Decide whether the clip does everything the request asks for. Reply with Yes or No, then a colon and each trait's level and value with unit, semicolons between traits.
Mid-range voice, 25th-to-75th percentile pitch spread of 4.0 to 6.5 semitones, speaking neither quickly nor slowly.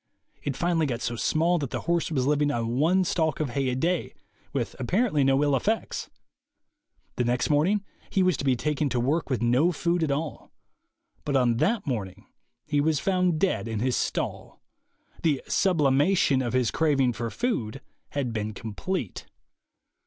Yes: medium, 145 Hz; average, 5.3 semitones; average, 175 wpm